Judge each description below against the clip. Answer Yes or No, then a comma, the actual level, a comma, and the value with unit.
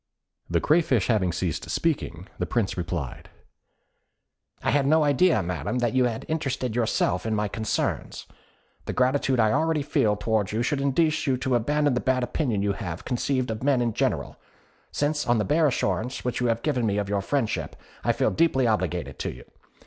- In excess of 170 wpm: Yes, average, 190 wpm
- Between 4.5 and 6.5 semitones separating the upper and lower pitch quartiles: Yes, average, 5.1 semitones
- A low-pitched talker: Yes, low, 120 Hz